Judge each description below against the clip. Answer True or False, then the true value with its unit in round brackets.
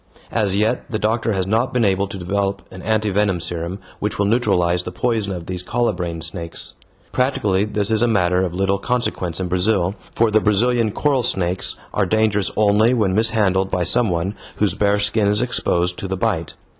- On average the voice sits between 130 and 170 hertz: False (100 Hz)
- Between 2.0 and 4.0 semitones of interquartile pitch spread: True (3.1 semitones)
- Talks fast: False (195 wpm)